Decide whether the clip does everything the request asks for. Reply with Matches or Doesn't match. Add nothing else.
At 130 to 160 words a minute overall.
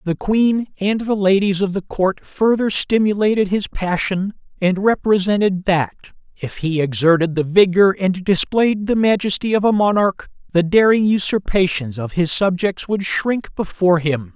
Matches